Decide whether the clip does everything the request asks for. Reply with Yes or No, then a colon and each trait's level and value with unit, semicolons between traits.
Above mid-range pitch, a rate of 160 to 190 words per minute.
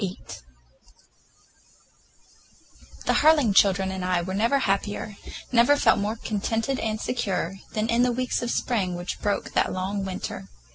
No: high, 210 Hz; average, 145 wpm